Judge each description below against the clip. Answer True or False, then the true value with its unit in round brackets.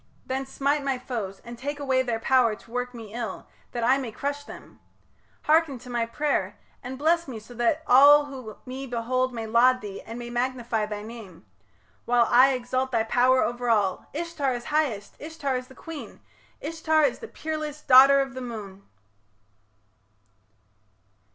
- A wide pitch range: False (3.2 semitones)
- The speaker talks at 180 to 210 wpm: False (170 wpm)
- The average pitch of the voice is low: False (255 Hz)